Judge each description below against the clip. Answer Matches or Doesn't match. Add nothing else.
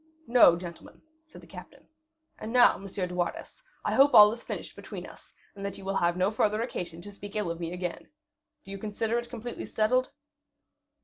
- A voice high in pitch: Matches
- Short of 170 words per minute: Doesn't match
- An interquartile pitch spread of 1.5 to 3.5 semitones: Doesn't match